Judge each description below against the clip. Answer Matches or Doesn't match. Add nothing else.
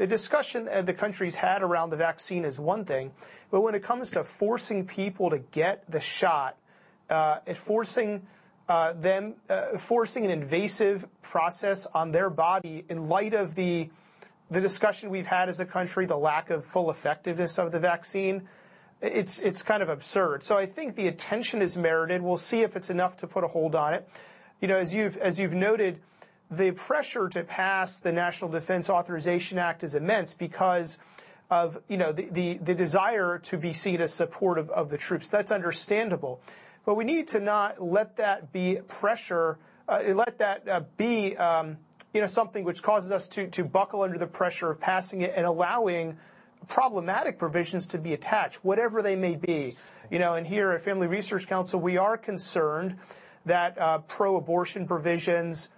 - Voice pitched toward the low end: Doesn't match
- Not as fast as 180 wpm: Doesn't match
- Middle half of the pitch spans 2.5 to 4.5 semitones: Matches